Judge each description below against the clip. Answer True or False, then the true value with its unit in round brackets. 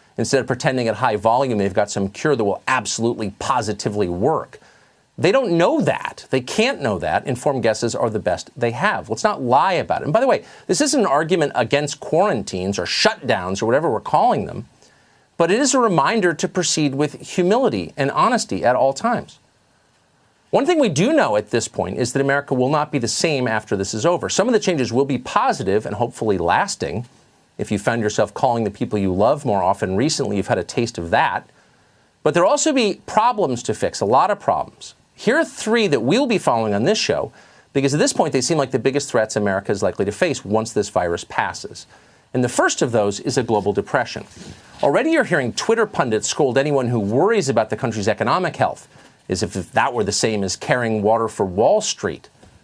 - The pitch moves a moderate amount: False (6.0 semitones)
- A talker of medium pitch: False (130 Hz)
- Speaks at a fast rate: True (215 wpm)